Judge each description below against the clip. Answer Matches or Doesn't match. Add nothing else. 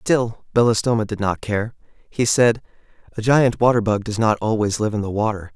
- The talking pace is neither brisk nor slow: Matches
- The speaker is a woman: Doesn't match